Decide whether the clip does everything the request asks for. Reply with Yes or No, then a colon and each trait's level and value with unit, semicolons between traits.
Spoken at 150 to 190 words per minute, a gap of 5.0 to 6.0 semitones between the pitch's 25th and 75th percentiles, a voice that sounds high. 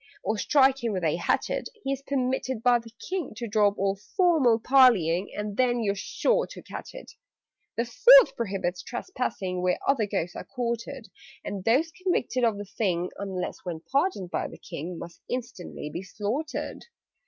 Yes: average, 170 wpm; wide, 5.6 semitones; high, 230 Hz